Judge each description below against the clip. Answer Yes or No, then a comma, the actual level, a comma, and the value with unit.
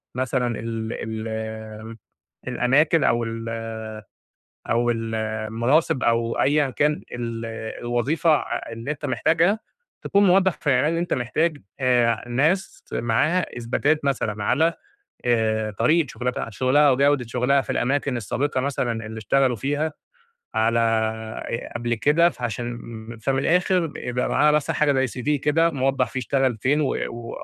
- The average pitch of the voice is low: Yes, low, 125 Hz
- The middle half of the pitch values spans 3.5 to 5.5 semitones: Yes, average, 4.4 semitones